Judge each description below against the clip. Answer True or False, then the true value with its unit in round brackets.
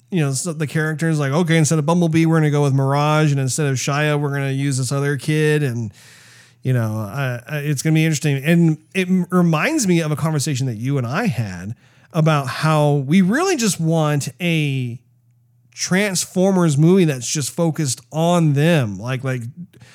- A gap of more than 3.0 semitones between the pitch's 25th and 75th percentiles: True (3.4 semitones)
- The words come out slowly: False (190 wpm)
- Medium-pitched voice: True (150 Hz)